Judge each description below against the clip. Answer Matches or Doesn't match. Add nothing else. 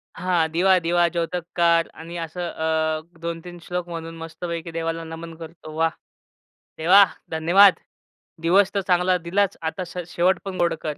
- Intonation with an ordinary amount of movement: Doesn't match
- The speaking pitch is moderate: Matches